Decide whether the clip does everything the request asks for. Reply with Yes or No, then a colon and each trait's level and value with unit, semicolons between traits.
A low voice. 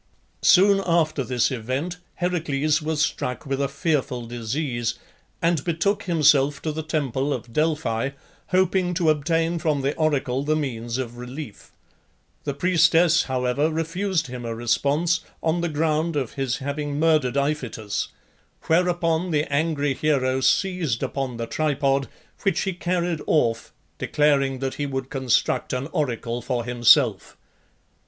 No: medium, 145 Hz